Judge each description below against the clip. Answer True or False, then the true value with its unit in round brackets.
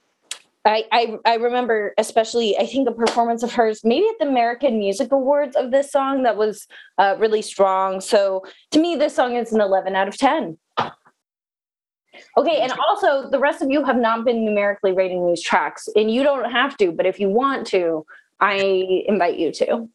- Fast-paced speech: False (195 wpm)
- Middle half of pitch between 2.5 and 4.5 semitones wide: False (5.3 semitones)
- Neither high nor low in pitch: False (230 Hz)